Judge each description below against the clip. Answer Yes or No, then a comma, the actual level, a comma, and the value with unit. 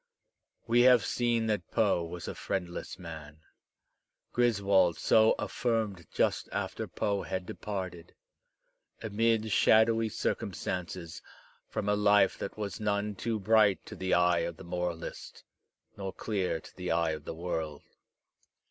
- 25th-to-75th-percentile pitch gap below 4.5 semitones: Yes, average, 3.9 semitones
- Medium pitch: No, low, 100 Hz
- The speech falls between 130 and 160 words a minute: Yes, average, 140 wpm